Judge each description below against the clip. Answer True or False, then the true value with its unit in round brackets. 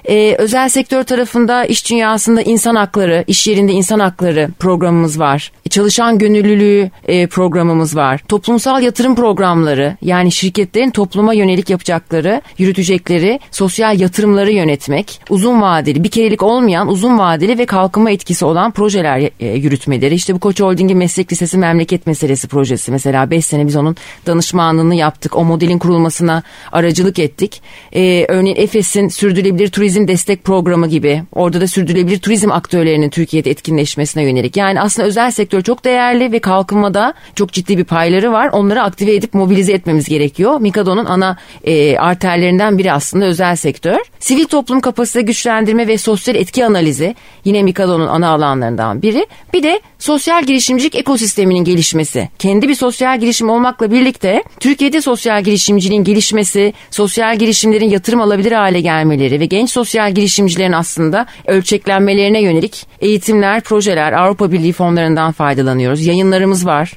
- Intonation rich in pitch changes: False (4.3 semitones)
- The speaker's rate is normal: False (145 wpm)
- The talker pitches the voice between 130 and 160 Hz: False (195 Hz)